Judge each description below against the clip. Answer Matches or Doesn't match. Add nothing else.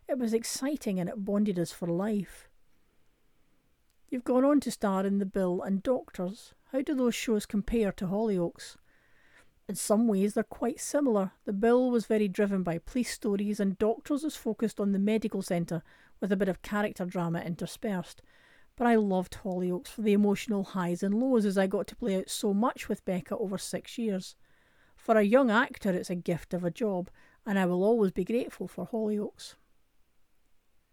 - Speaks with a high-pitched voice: Matches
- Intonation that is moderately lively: Matches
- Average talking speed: Matches